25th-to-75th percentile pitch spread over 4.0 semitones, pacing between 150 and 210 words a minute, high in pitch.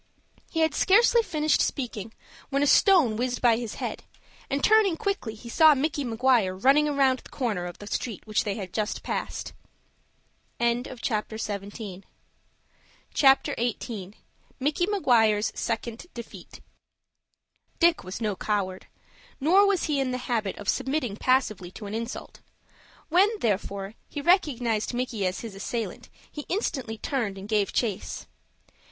No: wide, 5.4 semitones; average, 140 wpm; high, 240 Hz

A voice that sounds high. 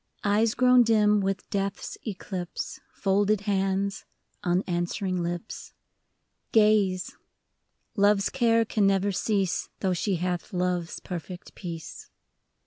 Yes: high, 195 Hz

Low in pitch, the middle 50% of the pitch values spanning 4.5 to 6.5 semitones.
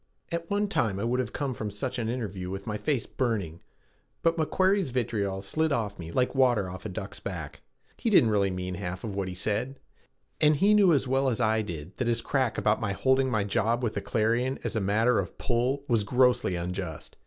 Yes: low, 115 Hz; average, 5.0 semitones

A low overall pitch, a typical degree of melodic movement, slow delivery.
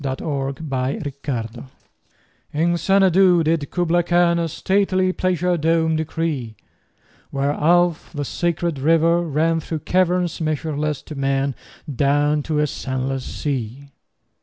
No: medium, 160 Hz; average, 3.5 semitones; slow, 115 wpm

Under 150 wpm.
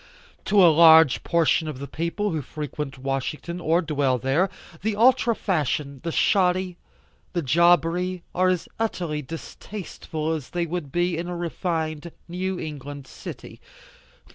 Yes: average, 140 wpm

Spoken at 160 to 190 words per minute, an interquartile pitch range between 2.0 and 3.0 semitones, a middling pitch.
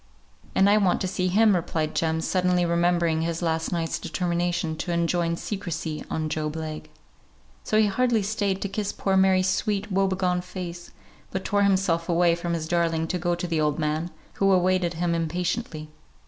Yes: average, 180 wpm; narrow, 2.4 semitones; medium, 175 Hz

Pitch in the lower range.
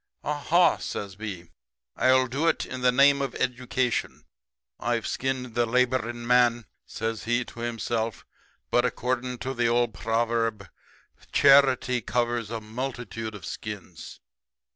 Yes: low, 120 Hz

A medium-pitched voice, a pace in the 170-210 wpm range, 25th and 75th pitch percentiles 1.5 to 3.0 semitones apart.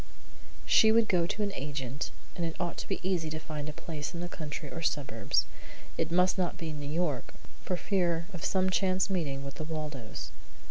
No: medium, 165 Hz; average, 200 wpm; average, 3.5 semitones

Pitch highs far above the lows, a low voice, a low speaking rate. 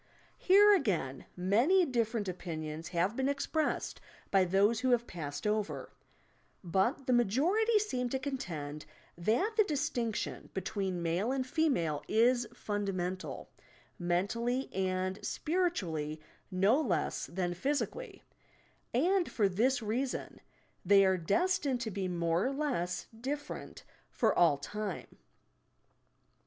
No: wide, 7.0 semitones; high, 215 Hz; slow, 125 wpm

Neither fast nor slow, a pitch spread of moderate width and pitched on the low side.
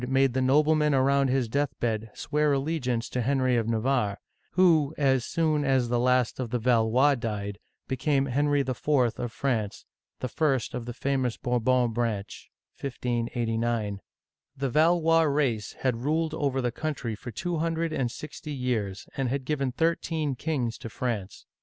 Yes: average, 155 wpm; average, 3.6 semitones; low, 130 Hz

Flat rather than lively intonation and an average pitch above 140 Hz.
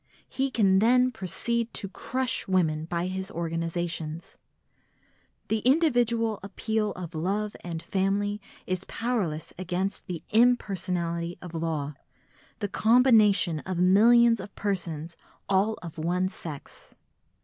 No: average, 4.6 semitones; high, 190 Hz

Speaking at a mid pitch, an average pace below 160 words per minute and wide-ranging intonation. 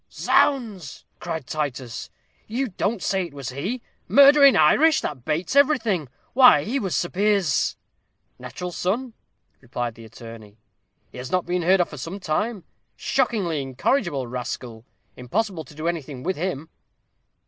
Yes: medium, 175 Hz; average, 150 wpm; wide, 8.2 semitones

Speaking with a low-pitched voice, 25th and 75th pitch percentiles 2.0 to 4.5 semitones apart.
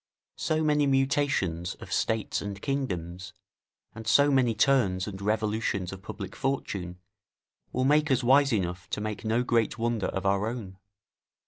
No: low, 110 Hz; wide, 5.6 semitones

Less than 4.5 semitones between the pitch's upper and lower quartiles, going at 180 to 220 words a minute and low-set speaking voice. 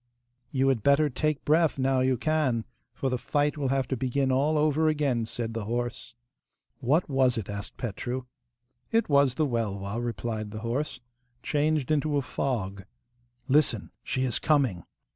No: average, 4.0 semitones; average, 160 wpm; low, 130 Hz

